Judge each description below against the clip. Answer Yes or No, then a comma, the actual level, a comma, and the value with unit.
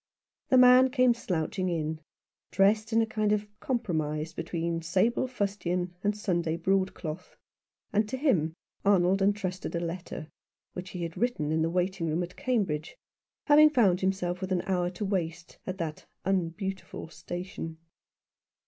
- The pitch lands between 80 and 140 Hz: No, medium, 185 Hz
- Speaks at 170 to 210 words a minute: No, average, 150 wpm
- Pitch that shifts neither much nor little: Yes, average, 3.8 semitones